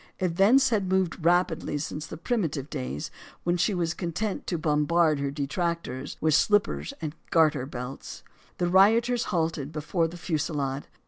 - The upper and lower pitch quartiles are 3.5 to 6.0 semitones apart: Yes, average, 3.9 semitones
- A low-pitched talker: No, medium, 165 Hz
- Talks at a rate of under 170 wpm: Yes, average, 145 wpm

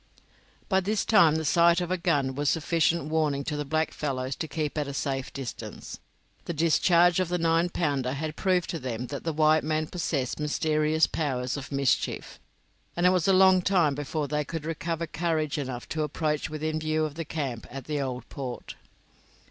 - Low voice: No, medium, 155 Hz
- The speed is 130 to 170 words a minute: No, average, 195 wpm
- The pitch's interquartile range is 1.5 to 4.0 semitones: Yes, average, 2.9 semitones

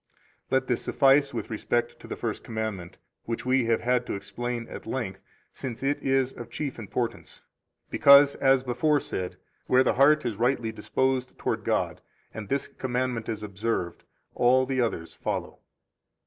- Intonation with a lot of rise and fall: No, average, 2.9 semitones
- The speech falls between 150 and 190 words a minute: Yes, average, 165 wpm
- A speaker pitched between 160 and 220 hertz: No, low, 125 Hz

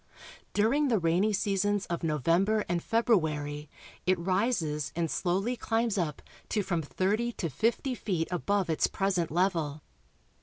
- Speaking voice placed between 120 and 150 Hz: No, medium, 185 Hz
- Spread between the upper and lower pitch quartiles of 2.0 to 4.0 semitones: No, average, 4.4 semitones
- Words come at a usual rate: Yes, average, 145 wpm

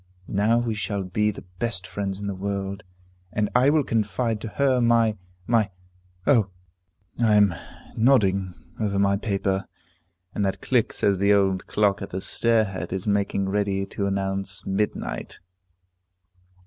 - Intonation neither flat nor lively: No, narrow, 2.3 semitones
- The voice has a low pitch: Yes, low, 100 Hz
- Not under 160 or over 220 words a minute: No, average, 150 wpm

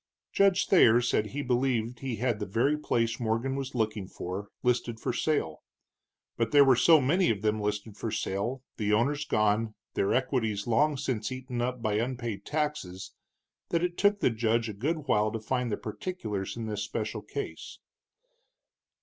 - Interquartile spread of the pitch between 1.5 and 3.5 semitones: No, average, 4.0 semitones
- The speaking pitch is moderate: No, low, 115 Hz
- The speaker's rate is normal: Yes, average, 175 wpm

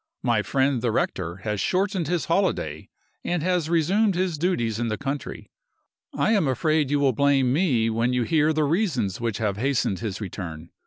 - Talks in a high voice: No, medium, 140 Hz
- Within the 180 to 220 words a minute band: Yes, average, 190 wpm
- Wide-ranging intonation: Yes, wide, 6.8 semitones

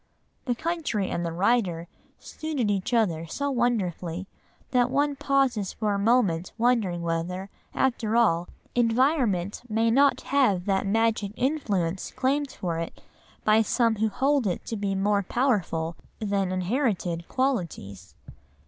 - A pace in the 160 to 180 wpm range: No, slow, 135 wpm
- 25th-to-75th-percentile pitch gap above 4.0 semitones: Yes, wide, 5.6 semitones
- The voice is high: Yes, high, 210 Hz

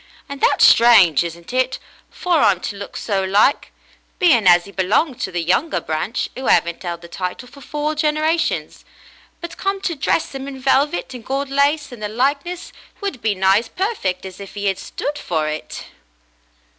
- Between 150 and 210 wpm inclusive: Yes, average, 185 wpm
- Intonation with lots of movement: Yes, wide, 7.4 semitones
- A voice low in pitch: No, high, 240 Hz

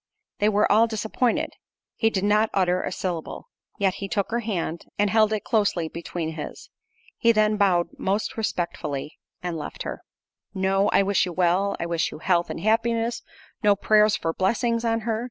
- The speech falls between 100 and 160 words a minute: No, average, 170 wpm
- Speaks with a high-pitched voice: Yes, high, 200 Hz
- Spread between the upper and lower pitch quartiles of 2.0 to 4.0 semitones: Yes, average, 3.7 semitones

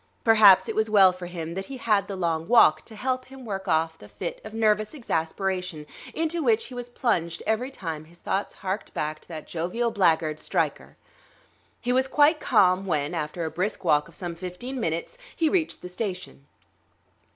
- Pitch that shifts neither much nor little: No, wide, 5.9 semitones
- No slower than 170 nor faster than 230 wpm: Yes, average, 195 wpm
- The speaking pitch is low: No, high, 190 Hz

